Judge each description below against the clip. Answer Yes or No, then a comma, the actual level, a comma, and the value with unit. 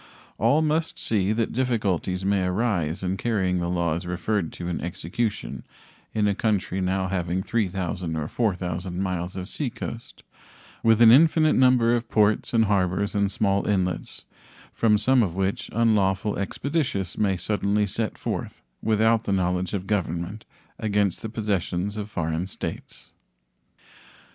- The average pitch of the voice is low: Yes, low, 100 Hz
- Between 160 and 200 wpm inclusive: No, average, 145 wpm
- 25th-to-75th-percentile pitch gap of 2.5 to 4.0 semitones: Yes, average, 3.4 semitones